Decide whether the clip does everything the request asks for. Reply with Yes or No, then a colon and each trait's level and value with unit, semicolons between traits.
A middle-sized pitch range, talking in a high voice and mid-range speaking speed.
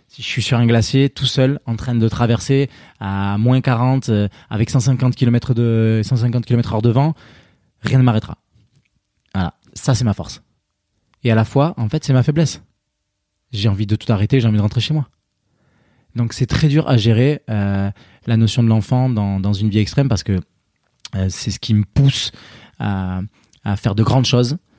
No: average, 3.4 semitones; low, 115 Hz; average, 200 wpm